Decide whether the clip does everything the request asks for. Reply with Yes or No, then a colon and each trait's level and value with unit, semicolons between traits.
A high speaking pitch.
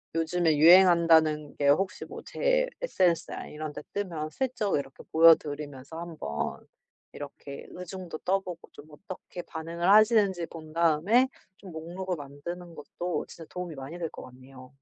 No: medium, 165 Hz